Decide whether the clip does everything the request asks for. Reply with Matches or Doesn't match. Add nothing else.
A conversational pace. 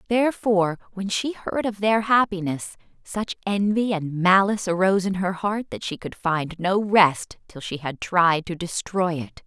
Matches